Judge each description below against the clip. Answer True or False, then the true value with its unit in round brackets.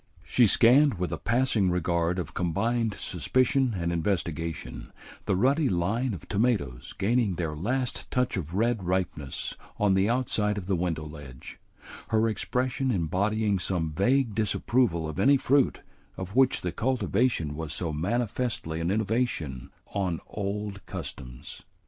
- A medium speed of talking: True (145 wpm)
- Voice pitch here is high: False (100 Hz)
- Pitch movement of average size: False (6.0 semitones)